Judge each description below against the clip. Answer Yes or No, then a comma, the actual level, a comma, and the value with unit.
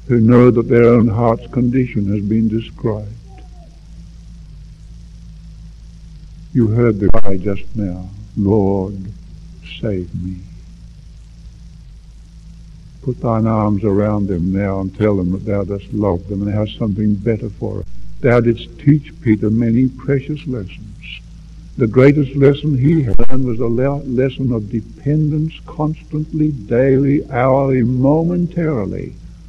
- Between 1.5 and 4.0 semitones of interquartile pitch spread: No, average, 4.6 semitones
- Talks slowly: Yes, slow, 125 wpm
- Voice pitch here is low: Yes, low, 115 Hz